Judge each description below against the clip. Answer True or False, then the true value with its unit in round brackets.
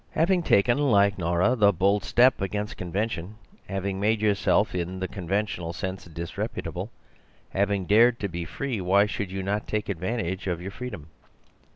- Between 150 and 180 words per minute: True (160 wpm)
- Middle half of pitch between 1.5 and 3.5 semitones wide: True (2.7 semitones)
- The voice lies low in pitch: True (100 Hz)